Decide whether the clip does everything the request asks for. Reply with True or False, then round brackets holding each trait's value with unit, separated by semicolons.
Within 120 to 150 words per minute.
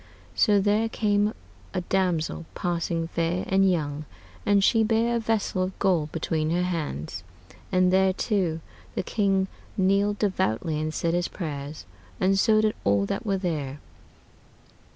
True (145 wpm)